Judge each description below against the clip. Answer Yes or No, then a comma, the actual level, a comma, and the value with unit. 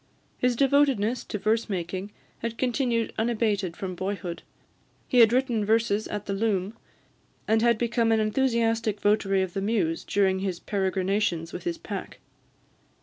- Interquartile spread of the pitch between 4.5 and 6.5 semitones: No, average, 3.2 semitones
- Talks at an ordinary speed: Yes, average, 145 wpm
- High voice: Yes, high, 215 Hz